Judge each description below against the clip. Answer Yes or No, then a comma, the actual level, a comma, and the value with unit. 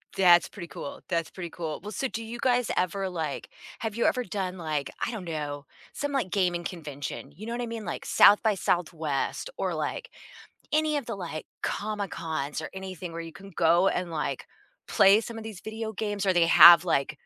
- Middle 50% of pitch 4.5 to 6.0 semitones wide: Yes, average, 4.8 semitones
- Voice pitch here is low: No, medium, 185 Hz